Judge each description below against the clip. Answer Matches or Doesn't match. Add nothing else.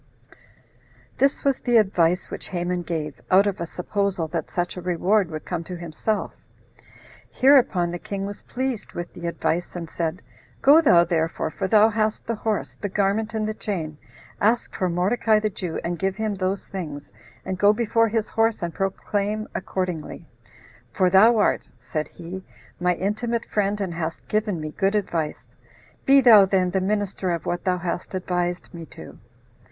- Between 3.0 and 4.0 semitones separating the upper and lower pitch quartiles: Matches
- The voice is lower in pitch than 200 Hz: Matches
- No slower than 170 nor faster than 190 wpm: Matches